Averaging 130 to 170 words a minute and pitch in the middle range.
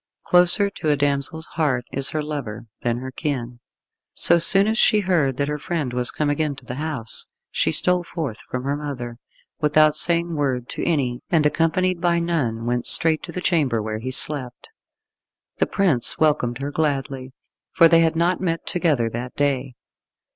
No: average, 180 wpm; medium, 145 Hz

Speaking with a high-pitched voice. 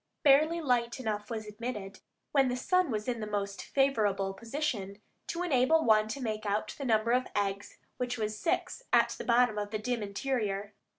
Yes: high, 225 Hz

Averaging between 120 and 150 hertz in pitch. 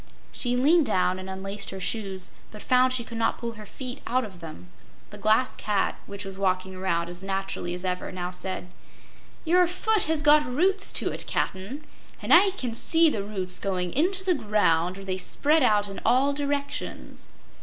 No: high, 210 Hz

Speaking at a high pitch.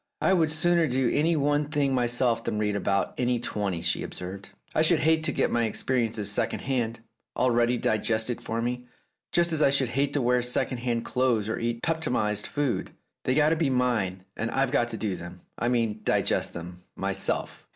No: low, 125 Hz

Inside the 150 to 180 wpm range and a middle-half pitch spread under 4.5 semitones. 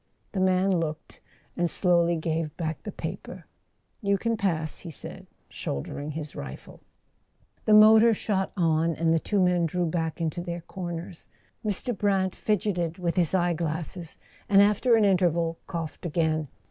Yes: average, 155 wpm; average, 2.9 semitones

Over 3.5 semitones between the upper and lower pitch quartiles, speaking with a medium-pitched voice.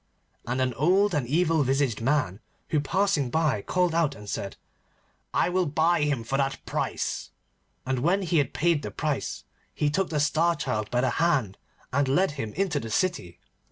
Yes: average, 4.7 semitones; medium, 145 Hz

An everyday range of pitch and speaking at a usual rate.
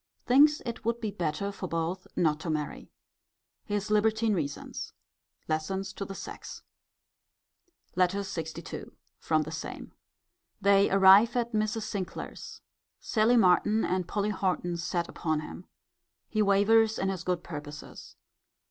No: average, 3.9 semitones; slow, 130 wpm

